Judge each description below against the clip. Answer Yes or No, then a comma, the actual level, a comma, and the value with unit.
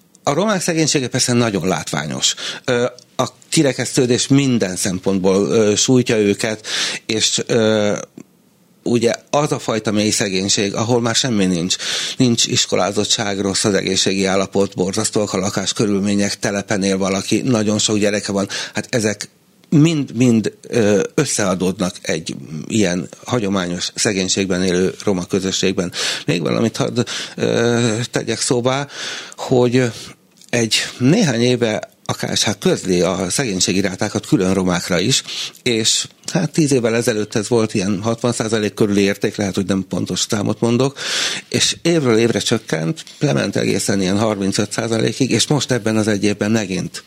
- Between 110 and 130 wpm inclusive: Yes, average, 125 wpm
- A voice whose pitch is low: Yes, low, 110 Hz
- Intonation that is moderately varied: Yes, average, 3.7 semitones